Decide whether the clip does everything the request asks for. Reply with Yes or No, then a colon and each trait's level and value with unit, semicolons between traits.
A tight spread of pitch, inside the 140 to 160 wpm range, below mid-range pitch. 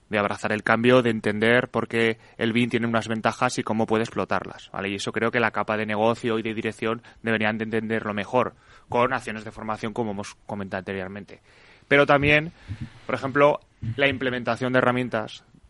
No: narrow, 2.2 semitones; average, 185 wpm; low, 115 Hz